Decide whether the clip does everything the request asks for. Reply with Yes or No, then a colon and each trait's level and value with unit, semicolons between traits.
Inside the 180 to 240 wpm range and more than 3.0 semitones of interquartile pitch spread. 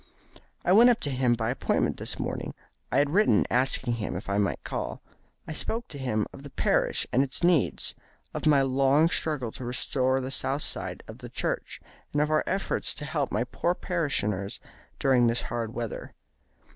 Yes: average, 190 wpm; average, 4.1 semitones